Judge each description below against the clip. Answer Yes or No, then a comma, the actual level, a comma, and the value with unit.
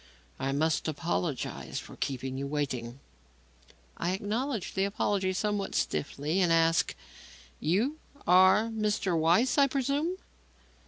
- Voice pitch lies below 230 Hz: Yes, medium, 185 Hz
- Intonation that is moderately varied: No, wide, 5.9 semitones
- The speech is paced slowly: Yes, slow, 115 wpm